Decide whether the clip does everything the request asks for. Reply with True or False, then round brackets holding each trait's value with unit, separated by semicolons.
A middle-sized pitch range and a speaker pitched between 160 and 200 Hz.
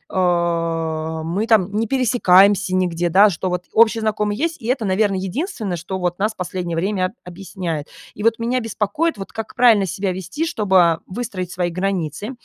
True (3.6 semitones; 190 Hz)